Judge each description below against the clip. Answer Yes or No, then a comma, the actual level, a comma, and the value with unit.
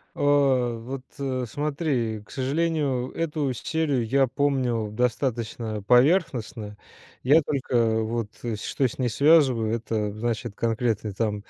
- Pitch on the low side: Yes, low, 125 Hz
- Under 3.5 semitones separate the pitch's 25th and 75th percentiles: No, average, 3.8 semitones